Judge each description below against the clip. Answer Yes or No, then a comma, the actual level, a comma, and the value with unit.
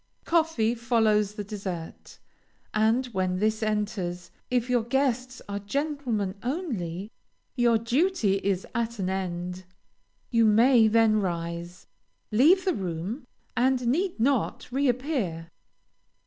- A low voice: No, high, 220 Hz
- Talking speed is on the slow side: Yes, slow, 120 wpm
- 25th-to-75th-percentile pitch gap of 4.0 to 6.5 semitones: Yes, average, 4.8 semitones